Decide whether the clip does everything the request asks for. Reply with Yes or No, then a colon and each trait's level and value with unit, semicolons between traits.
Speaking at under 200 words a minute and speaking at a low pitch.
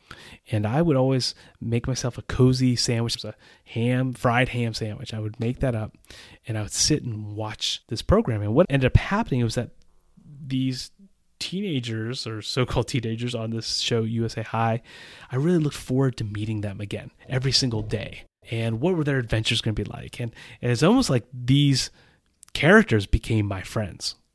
Yes: average, 190 wpm; low, 120 Hz